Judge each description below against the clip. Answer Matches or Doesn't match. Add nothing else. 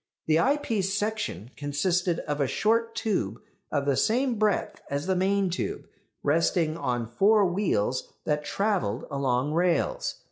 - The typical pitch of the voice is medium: Matches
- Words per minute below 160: Matches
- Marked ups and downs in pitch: Matches